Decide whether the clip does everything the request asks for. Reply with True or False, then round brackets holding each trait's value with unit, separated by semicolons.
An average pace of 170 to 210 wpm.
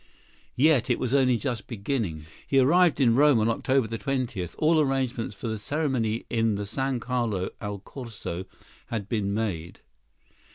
False (155 wpm)